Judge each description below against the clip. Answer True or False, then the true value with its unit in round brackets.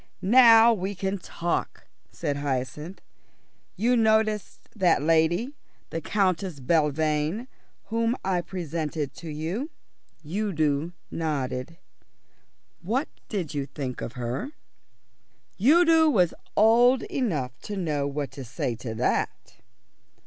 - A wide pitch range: True (6.7 semitones)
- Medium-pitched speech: True (170 Hz)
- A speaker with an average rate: False (110 wpm)